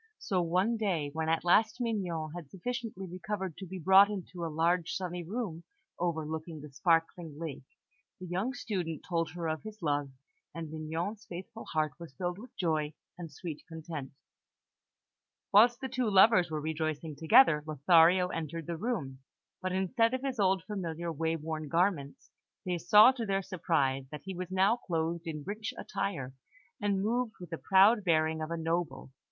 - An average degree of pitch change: Yes, average, 3.7 semitones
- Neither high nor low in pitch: Yes, medium, 175 Hz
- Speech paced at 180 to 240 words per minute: No, average, 170 wpm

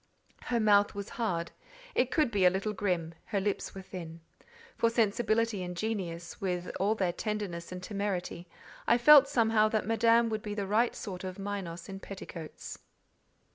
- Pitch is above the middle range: Yes, high, 200 Hz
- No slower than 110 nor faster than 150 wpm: No, average, 170 wpm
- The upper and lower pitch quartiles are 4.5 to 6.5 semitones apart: No, average, 3.5 semitones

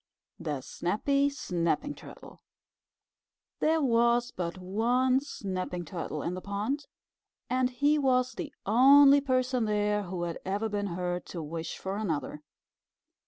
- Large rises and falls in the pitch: Yes, wide, 6.2 semitones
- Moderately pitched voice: No, high, 210 Hz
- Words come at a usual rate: No, slow, 130 wpm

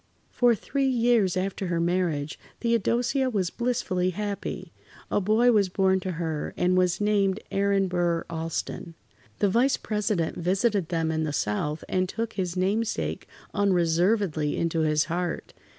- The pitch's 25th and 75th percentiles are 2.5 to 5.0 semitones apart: Yes, average, 3.9 semitones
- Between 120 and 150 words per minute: Yes, average, 145 wpm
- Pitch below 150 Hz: No, medium, 185 Hz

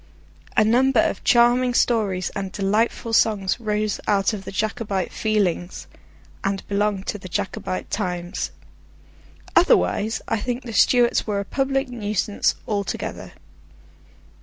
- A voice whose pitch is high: Yes, high, 210 Hz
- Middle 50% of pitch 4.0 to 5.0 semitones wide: No, average, 3.2 semitones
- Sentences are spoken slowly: Yes, slow, 125 wpm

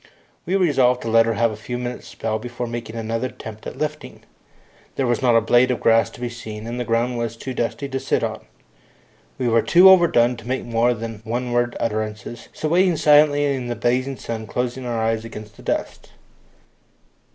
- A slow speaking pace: No, fast, 205 wpm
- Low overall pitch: Yes, low, 120 Hz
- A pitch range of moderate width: No, narrow, 2.1 semitones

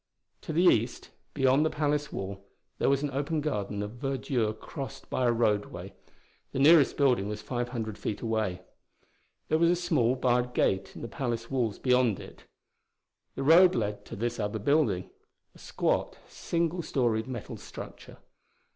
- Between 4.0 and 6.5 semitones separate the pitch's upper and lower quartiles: Yes, average, 4.9 semitones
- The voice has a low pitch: Yes, low, 125 Hz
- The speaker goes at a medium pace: Yes, average, 165 wpm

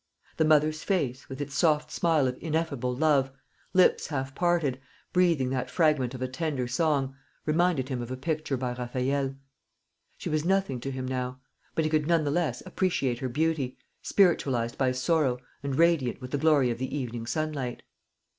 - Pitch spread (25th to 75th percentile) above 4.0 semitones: No, average, 3.7 semitones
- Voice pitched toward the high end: No, medium, 140 Hz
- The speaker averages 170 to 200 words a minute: Yes, average, 175 wpm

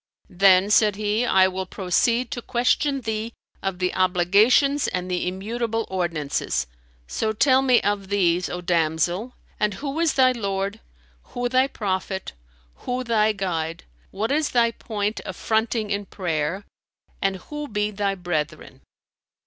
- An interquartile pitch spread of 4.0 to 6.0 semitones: Yes, average, 4.3 semitones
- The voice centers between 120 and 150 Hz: No, high, 205 Hz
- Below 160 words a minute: Yes, average, 145 wpm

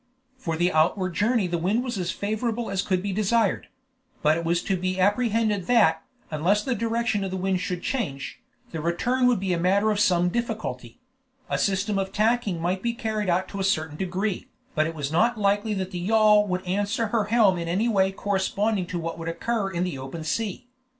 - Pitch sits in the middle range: No, high, 195 Hz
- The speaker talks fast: Yes, fast, 210 wpm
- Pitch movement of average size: Yes, average, 3.7 semitones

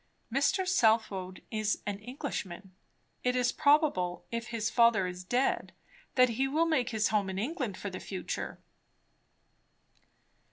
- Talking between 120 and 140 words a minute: Yes, slow, 135 wpm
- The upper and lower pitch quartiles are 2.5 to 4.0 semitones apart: No, average, 5.1 semitones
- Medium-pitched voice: No, high, 230 Hz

